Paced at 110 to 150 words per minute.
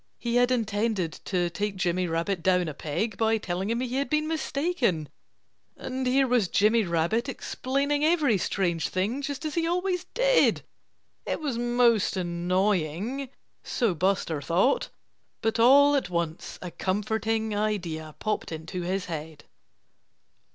Yes: average, 145 wpm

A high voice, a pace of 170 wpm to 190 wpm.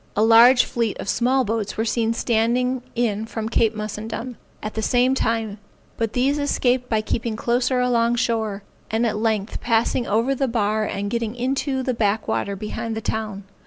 Yes: high, 230 Hz; average, 180 wpm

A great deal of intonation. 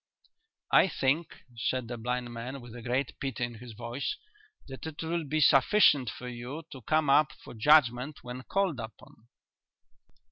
No: average, 3.7 semitones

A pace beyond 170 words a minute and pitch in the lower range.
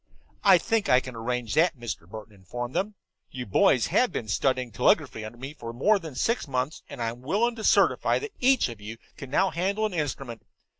Yes: fast, 205 wpm; low, 130 Hz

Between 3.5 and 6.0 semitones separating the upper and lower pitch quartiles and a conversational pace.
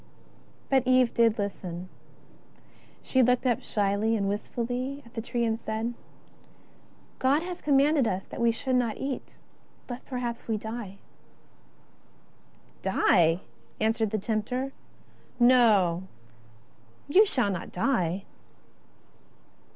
No: average, 3.9 semitones; slow, 125 wpm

